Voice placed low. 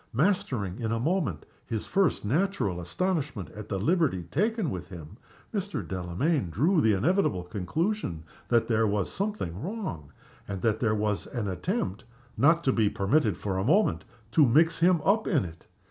Yes: low, 115 Hz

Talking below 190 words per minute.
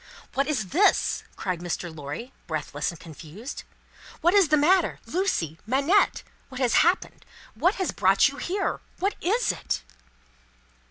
Yes: average, 145 wpm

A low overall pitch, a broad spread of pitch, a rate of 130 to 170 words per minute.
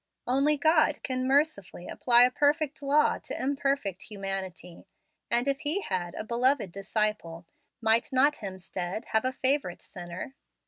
No: high, 245 Hz; wide, 6.5 semitones; average, 140 wpm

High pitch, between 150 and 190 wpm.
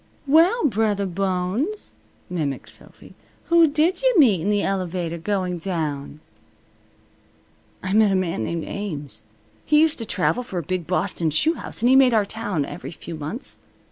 Yes: high, 195 Hz; average, 165 wpm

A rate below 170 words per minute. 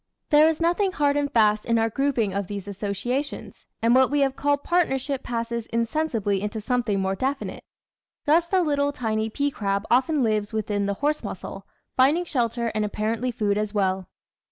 No: average, 180 wpm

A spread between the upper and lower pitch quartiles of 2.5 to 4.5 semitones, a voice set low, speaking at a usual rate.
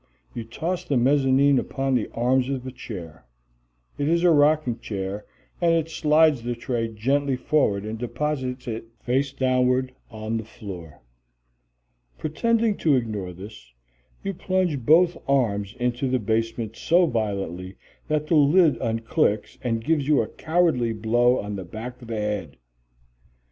No: average, 5.0 semitones; low, 125 Hz; average, 150 wpm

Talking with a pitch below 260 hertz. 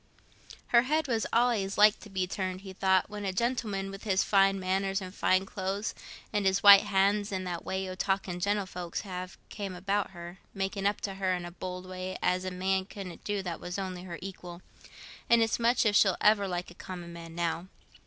Yes: high, 190 Hz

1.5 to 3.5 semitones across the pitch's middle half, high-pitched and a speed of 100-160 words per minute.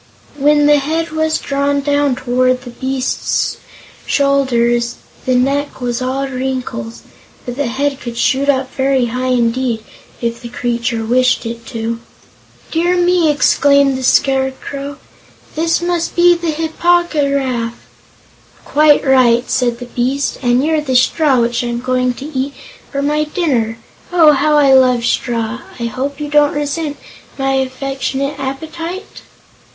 Yes: average, 3.0 semitones; very high, 270 Hz; average, 145 wpm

